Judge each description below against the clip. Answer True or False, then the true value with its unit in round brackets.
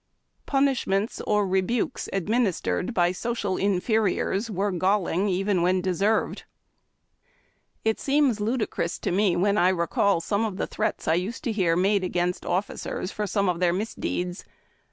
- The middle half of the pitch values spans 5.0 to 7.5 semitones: False (3.1 semitones)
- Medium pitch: False (195 Hz)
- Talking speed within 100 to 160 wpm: True (140 wpm)